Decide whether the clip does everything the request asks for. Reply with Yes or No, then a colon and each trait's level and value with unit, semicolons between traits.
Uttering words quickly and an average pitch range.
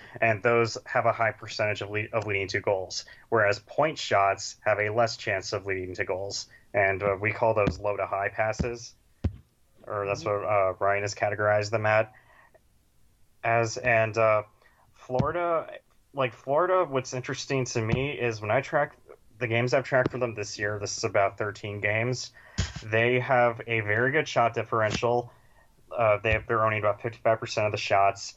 No: average, 180 wpm; average, 3.0 semitones